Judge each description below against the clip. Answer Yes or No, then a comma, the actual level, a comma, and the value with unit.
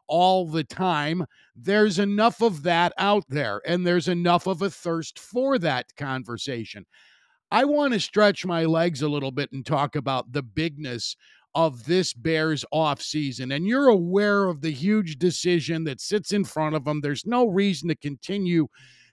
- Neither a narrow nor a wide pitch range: Yes, average, 5.0 semitones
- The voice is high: No, medium, 165 Hz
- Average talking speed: Yes, average, 175 wpm